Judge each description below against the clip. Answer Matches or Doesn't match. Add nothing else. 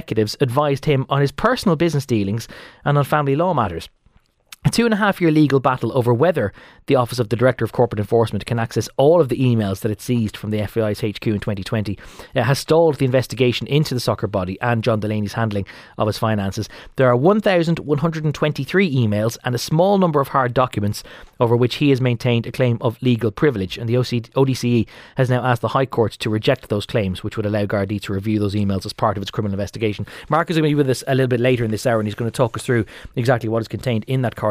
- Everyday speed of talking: Doesn't match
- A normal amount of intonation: Matches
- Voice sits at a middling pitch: Doesn't match